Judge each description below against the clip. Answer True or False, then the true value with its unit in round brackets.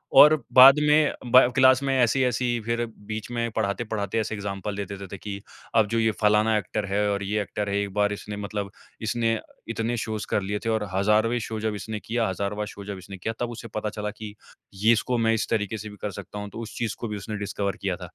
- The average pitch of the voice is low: True (105 Hz)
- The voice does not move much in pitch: True (2.1 semitones)